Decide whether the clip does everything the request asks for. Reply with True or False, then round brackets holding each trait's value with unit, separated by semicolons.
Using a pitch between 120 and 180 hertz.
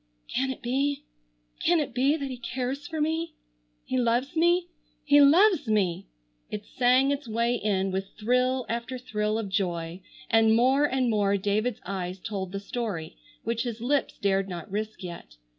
False (235 Hz)